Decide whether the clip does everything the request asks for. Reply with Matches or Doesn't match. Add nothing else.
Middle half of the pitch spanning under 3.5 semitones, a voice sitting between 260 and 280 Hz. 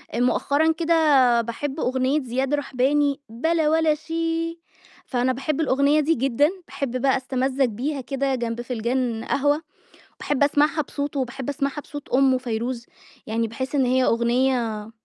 Matches